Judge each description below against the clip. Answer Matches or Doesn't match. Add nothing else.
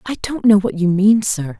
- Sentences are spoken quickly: Matches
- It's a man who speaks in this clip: Doesn't match